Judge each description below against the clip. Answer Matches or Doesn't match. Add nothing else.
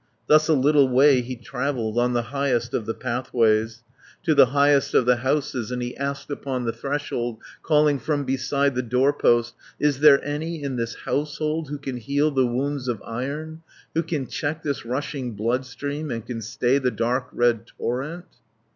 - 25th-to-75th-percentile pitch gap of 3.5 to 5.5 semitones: Doesn't match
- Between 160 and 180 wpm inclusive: Matches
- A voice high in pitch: Doesn't match